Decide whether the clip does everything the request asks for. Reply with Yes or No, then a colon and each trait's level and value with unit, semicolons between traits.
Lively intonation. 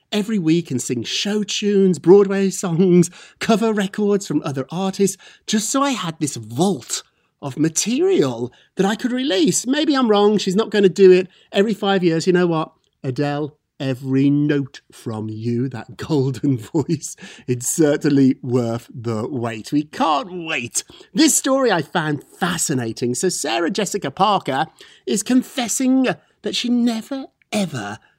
Yes: wide, 7.0 semitones